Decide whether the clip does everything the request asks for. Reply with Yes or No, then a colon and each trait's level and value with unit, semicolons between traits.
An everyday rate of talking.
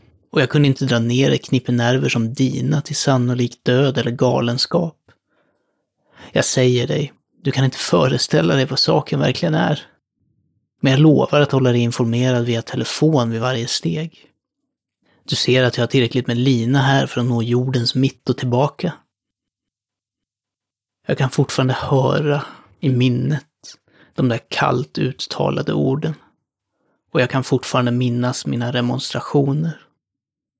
Yes: average, 145 wpm